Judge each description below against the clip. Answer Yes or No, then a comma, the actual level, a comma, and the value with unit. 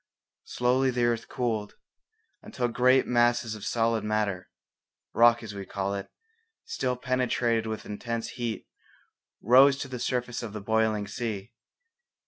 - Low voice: Yes, low, 115 Hz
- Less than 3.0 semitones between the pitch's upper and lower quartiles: Yes, narrow, 2.4 semitones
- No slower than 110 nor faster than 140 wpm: Yes, slow, 135 wpm